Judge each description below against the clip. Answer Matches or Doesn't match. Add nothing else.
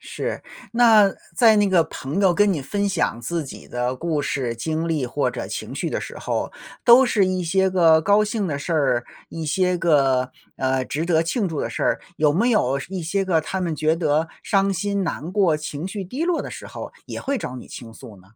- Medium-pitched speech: Matches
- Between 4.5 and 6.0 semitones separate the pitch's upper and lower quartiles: Matches